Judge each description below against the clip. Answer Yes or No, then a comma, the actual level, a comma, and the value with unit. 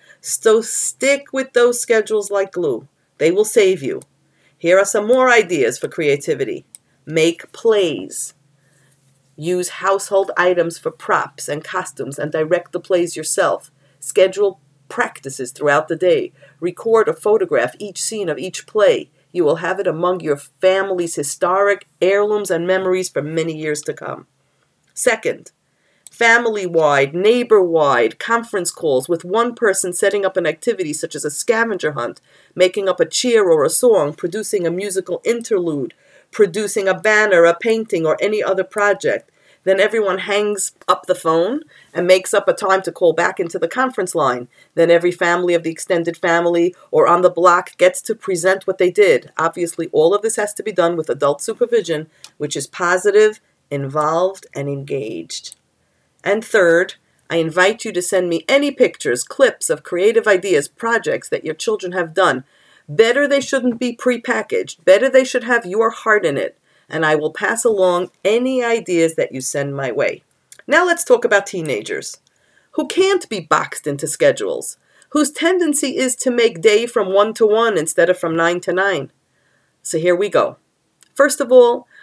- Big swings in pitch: Yes, wide, 6.3 semitones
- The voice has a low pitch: No, high, 195 Hz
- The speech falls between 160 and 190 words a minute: Yes, average, 170 wpm